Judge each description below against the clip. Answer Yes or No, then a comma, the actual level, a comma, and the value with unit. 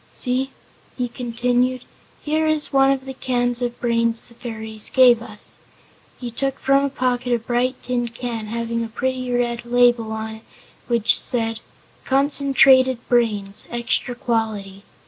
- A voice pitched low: No, high, 245 Hz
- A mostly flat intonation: Yes, narrow, 1.9 semitones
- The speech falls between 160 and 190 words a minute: No, average, 145 wpm